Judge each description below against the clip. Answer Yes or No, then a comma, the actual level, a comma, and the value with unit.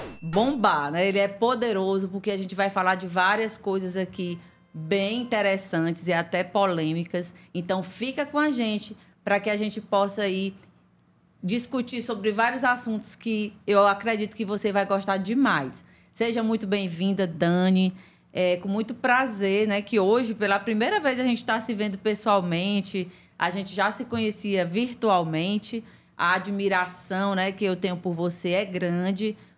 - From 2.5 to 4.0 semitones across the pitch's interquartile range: Yes, average, 2.9 semitones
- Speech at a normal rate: Yes, average, 160 wpm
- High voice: Yes, high, 200 Hz